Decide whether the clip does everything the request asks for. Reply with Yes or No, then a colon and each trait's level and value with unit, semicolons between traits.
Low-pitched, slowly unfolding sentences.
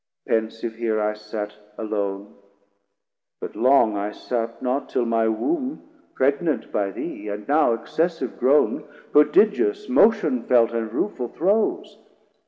Yes: low, 120 Hz; slow, 125 wpm